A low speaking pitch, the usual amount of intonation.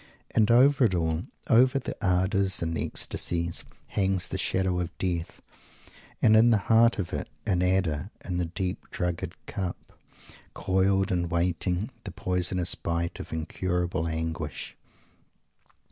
No: very low, 90 Hz; narrow, 2.3 semitones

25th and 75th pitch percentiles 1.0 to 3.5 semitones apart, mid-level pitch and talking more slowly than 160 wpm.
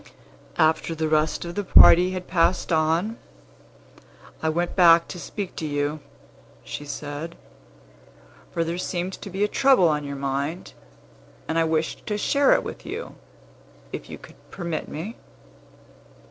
Yes: average, 2.9 semitones; medium, 165 Hz; average, 150 wpm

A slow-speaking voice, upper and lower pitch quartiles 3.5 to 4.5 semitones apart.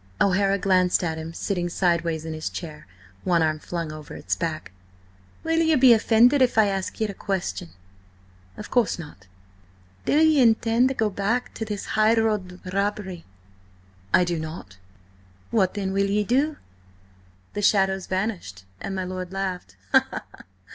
No: average, 155 wpm; average, 4.2 semitones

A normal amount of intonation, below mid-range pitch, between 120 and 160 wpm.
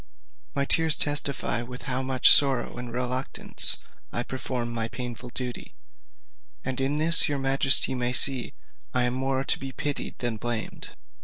No: narrow, 1.9 semitones; low, 130 Hz; average, 155 wpm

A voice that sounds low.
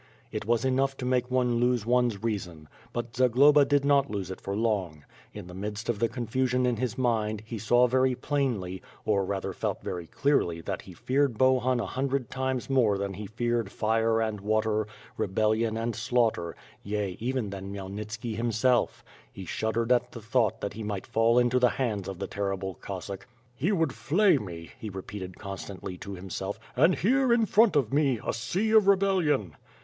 Yes: low, 115 Hz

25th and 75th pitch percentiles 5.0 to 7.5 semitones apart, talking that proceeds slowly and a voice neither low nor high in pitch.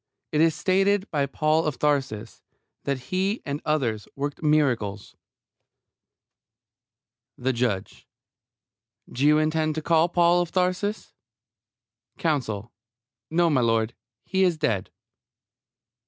Yes: average, 5.3 semitones; slow, 110 wpm; medium, 150 Hz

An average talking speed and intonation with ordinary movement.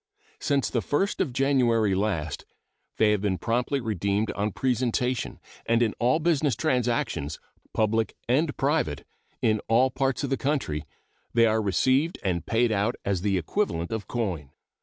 Yes: average, 155 wpm; average, 4.7 semitones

